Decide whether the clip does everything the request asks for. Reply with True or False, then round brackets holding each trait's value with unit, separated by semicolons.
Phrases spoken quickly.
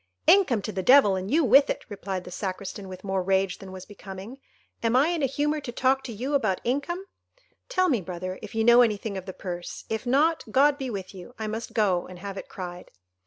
True (225 wpm)